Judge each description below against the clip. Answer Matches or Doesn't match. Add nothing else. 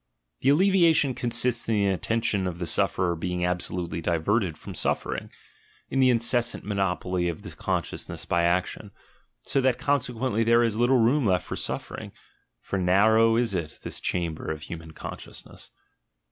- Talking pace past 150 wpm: Matches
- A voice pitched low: Matches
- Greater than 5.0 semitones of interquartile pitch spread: Matches